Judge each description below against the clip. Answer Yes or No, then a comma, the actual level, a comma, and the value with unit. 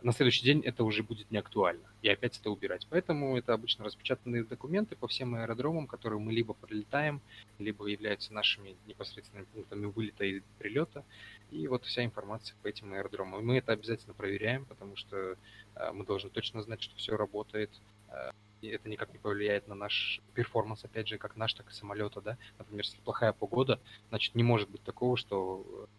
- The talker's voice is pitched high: No, low, 110 Hz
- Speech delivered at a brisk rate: Yes, fast, 180 wpm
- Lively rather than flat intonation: No, narrow, 2.6 semitones